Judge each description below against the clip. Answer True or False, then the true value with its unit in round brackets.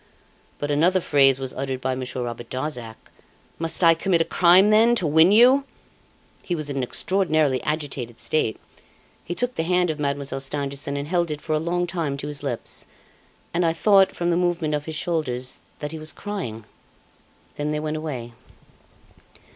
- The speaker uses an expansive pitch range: False (4.1 semitones)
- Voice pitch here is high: False (155 Hz)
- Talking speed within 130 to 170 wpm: False (180 wpm)